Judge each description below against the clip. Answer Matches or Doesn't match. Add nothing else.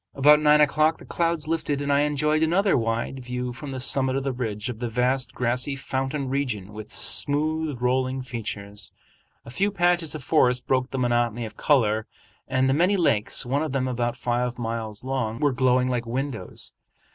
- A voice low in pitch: Matches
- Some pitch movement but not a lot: Matches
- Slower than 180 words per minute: Doesn't match